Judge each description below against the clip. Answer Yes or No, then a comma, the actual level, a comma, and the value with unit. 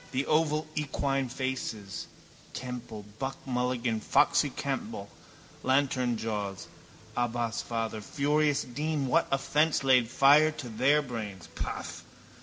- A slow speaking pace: Yes, slow, 105 wpm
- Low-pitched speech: Yes, low, 130 Hz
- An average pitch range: Yes, average, 3.6 semitones